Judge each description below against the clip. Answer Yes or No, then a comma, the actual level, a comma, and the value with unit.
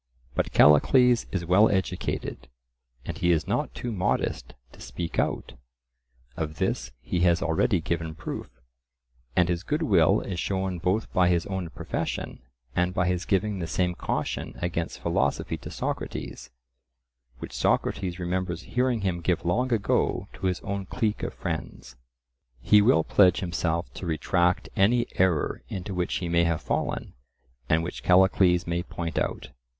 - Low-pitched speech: Yes, very low, 90 Hz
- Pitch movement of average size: No, narrow, 2.2 semitones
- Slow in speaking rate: No, average, 155 wpm